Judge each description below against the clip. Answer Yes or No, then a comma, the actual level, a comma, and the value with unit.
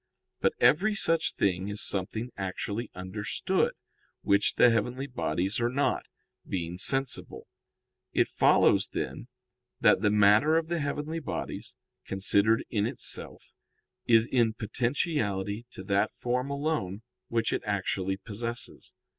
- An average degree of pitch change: Yes, average, 5.0 semitones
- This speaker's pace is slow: Yes, slow, 125 wpm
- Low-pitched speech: Yes, low, 115 Hz